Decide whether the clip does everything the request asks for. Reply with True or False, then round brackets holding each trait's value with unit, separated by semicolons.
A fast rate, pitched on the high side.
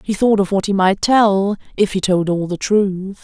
True (225 wpm; 195 Hz)